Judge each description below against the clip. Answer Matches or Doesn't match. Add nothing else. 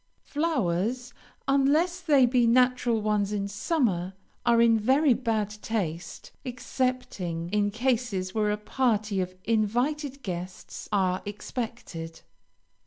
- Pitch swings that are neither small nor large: Matches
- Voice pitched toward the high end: Matches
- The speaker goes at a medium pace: Doesn't match